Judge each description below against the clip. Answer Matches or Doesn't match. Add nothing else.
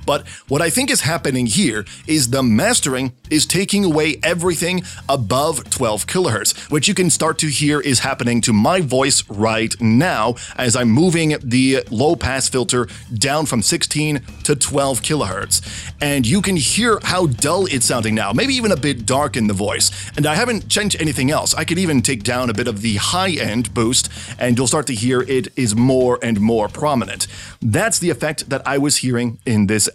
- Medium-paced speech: Matches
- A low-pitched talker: Matches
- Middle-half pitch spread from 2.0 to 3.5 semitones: Doesn't match